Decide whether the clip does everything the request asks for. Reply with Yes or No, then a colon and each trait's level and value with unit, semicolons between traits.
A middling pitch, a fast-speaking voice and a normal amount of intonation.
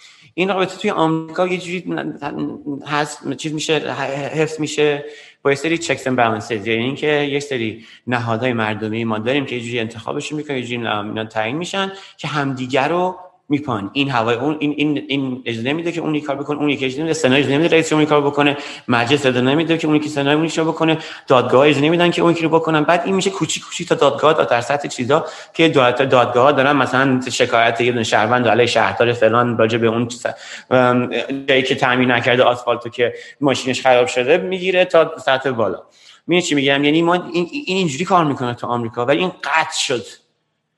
Yes: medium, 145 Hz; fast, 190 wpm; average, 4.6 semitones